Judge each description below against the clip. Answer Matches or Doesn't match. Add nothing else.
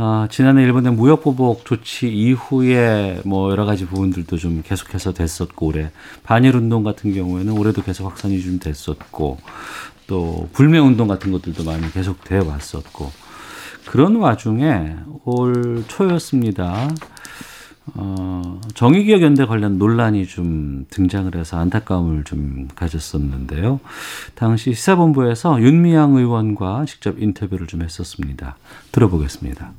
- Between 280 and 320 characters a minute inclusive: Matches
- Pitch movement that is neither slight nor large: Doesn't match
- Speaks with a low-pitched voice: Matches